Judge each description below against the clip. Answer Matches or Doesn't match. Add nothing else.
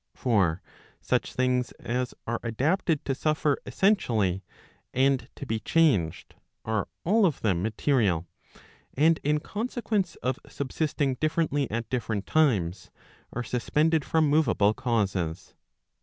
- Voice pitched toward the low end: Matches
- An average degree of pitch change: Doesn't match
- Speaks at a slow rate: Matches